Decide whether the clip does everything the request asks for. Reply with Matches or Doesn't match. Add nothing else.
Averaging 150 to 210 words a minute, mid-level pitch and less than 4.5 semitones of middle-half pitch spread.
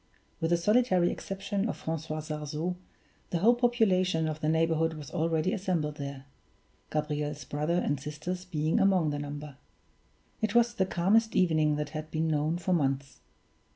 Matches